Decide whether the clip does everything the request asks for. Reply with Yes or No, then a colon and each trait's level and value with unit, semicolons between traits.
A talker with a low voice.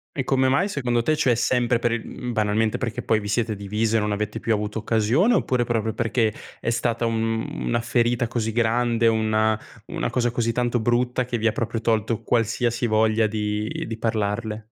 Yes: low, 115 Hz